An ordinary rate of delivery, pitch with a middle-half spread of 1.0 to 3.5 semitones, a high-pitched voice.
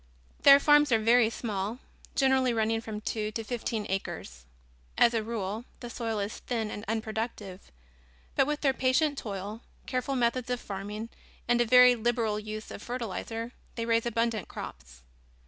Yes: average, 160 wpm; narrow, 2.5 semitones; high, 230 Hz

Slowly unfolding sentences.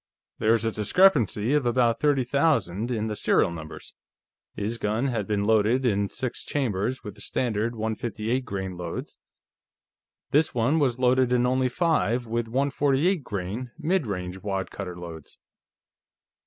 No: average, 150 wpm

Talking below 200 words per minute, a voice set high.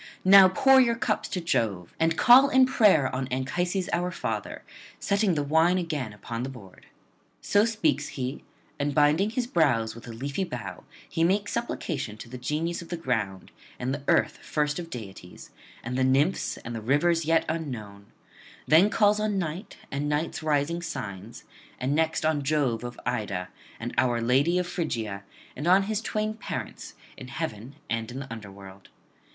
No: average, 175 wpm; medium, 150 Hz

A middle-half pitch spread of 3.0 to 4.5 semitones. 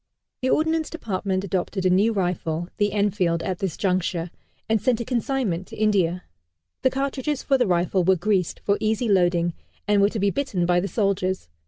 Yes: average, 3.7 semitones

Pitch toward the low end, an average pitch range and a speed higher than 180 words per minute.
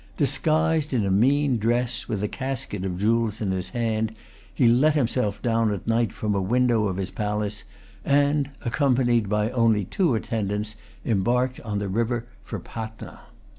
No: low, 115 Hz; average, 3.3 semitones; average, 165 wpm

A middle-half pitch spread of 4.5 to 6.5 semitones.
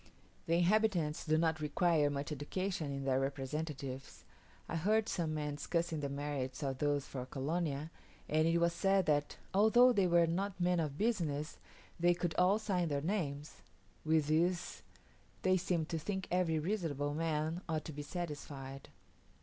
No: average, 3.5 semitones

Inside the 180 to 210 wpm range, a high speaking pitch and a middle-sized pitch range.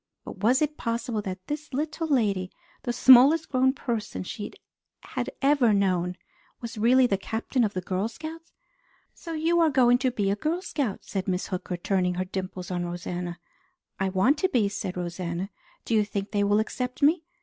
No: average, 185 wpm; high, 220 Hz; wide, 5.9 semitones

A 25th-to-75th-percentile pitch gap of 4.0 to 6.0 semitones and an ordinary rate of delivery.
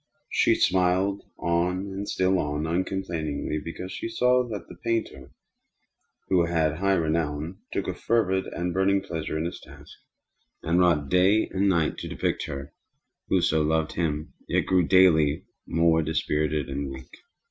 No: average, 3.4 semitones; average, 160 wpm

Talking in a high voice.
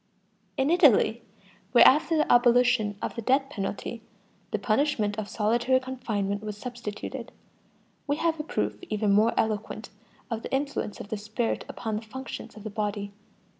Yes: high, 225 Hz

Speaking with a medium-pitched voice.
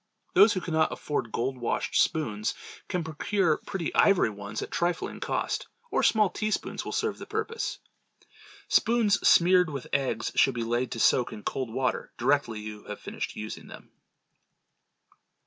Yes: medium, 145 Hz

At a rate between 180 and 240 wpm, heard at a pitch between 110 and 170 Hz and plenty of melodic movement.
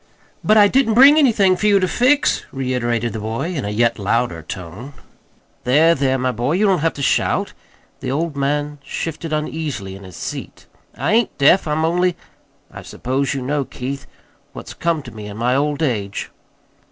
Yes: average, 185 wpm; medium, 140 Hz; wide, 5.9 semitones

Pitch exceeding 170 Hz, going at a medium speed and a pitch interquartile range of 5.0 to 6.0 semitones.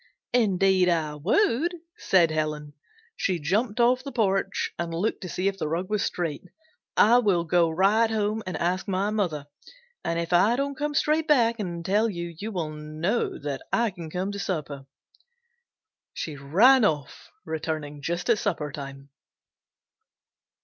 Yes: medium, 185 Hz; average, 160 wpm; average, 5.3 semitones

